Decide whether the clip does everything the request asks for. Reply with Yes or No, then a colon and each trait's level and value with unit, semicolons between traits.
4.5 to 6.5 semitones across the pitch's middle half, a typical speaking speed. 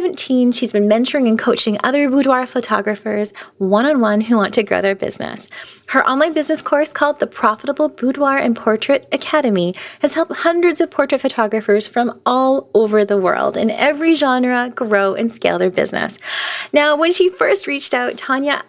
Yes: average, 5.2 semitones; average, 175 wpm